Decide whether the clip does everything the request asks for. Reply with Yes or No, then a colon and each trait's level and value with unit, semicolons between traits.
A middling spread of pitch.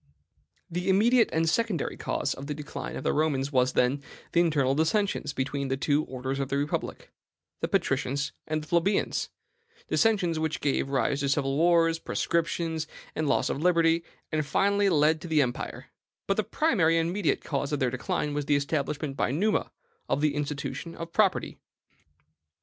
Yes: average, 3.3 semitones